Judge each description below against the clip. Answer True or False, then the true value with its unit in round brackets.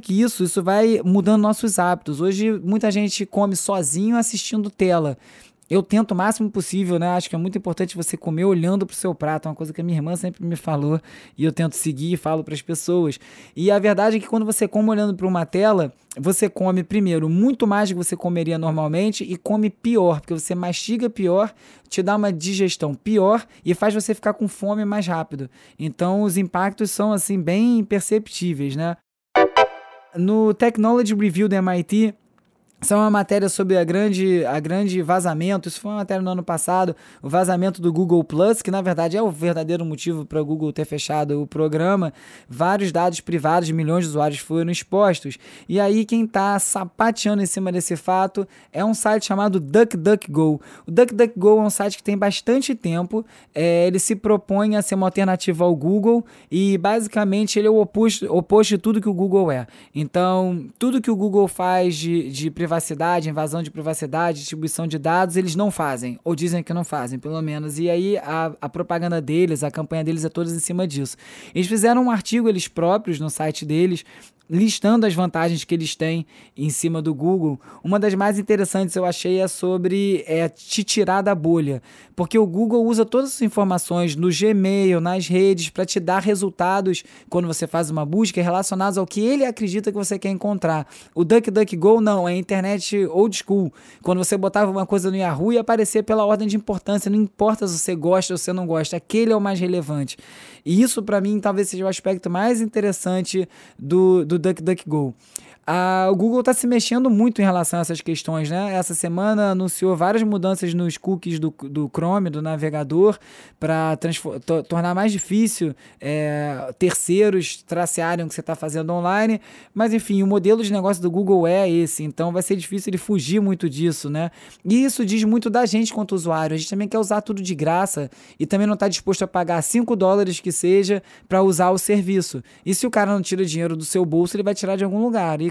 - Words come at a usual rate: False (200 wpm)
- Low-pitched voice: False (185 Hz)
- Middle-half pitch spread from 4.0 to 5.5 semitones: False (3.6 semitones)